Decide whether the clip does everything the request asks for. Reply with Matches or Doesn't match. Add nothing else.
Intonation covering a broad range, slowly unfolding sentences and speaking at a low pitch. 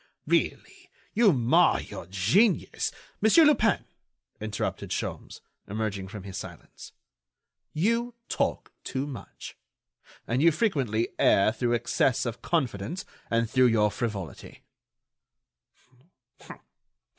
Matches